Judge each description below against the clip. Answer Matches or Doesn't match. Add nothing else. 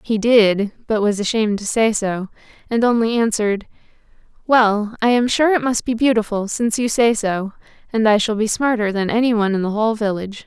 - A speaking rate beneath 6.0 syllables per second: Matches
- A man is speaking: Doesn't match